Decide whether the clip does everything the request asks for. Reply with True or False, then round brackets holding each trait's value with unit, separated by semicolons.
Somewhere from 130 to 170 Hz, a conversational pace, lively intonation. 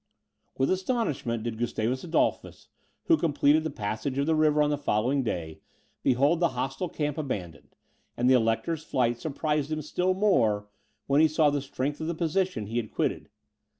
False (140 Hz; 175 wpm; 4.9 semitones)